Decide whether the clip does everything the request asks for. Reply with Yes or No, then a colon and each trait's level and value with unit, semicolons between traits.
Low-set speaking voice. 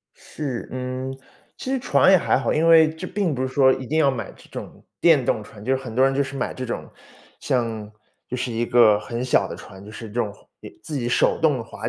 Yes: low, 130 Hz